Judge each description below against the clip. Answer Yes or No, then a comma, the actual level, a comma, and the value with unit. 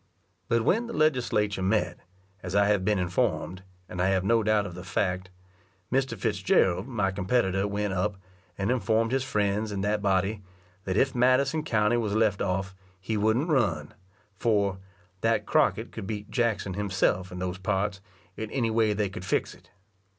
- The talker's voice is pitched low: Yes, low, 105 Hz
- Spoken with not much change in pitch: No, average, 3.0 semitones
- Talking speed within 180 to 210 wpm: No, average, 170 wpm